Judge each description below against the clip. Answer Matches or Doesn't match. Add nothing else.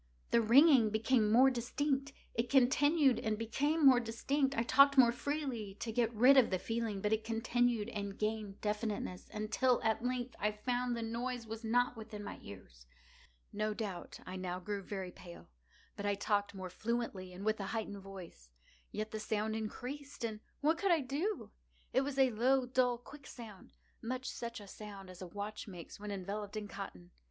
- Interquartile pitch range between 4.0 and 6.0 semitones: Doesn't match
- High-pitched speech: Matches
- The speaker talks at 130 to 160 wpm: Doesn't match